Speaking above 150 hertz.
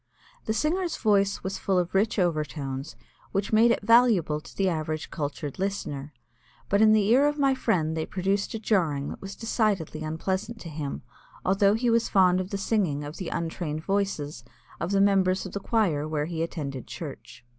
Yes: high, 190 Hz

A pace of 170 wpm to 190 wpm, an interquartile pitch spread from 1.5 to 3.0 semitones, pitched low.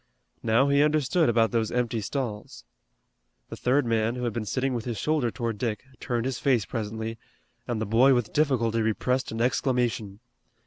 Yes: average, 175 wpm; narrow, 2.6 semitones; low, 120 Hz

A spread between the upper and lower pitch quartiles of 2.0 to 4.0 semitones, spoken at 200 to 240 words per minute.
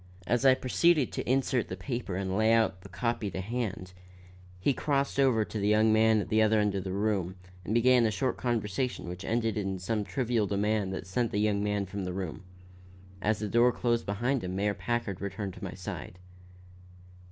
Yes: average, 3.5 semitones; fast, 205 wpm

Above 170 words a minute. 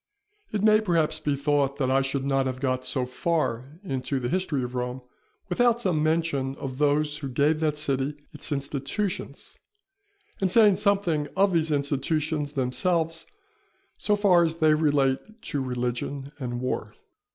No: average, 155 wpm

